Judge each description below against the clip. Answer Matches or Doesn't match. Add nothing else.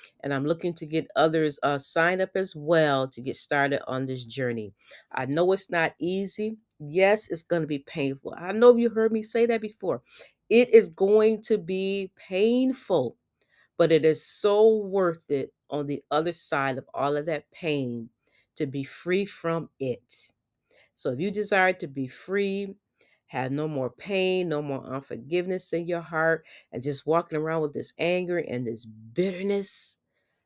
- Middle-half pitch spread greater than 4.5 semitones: Matches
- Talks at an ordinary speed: Matches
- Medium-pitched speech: Matches